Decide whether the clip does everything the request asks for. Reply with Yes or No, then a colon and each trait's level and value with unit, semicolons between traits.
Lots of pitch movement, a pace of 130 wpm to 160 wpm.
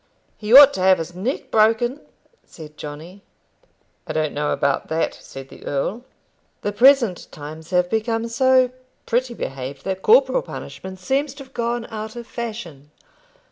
Yes: wide, 7.0 semitones; average, 155 wpm